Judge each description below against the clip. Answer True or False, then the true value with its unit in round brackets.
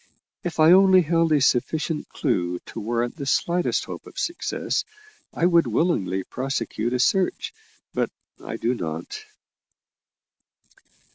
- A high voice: False (140 Hz)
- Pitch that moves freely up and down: True (6.6 semitones)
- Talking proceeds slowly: True (130 wpm)